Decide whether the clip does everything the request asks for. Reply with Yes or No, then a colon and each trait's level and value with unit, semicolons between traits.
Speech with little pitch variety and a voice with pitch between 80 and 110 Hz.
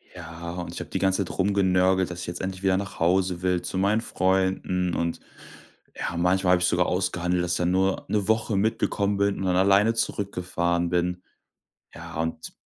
Yes: narrow, 1.6 semitones; very low, 95 Hz